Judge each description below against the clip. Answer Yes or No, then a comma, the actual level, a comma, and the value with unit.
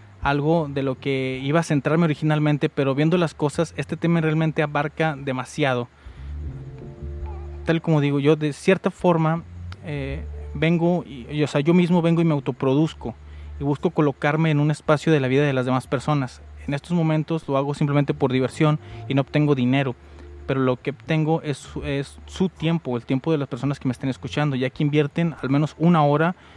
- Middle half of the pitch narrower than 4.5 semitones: Yes, average, 3.3 semitones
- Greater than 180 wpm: Yes, fast, 190 wpm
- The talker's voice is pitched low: No, medium, 145 Hz